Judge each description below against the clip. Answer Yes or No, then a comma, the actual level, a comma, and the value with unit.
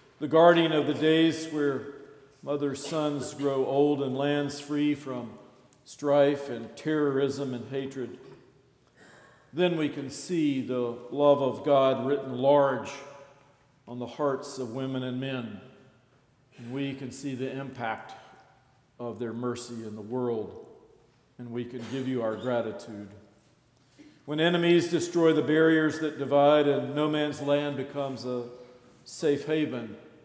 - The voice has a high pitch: No, medium, 140 Hz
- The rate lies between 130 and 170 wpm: Yes, slow, 135 wpm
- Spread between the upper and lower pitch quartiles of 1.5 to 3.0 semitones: Yes, narrow, 2.6 semitones